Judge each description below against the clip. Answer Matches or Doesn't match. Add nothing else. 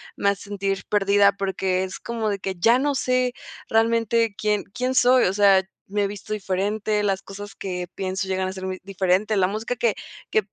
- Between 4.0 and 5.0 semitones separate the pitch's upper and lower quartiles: Doesn't match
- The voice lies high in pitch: Matches